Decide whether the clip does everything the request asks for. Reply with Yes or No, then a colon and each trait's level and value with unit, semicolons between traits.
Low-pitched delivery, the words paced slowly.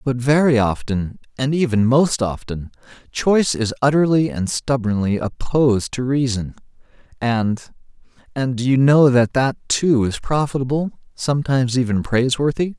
Yes: low, 130 Hz; slow, 130 wpm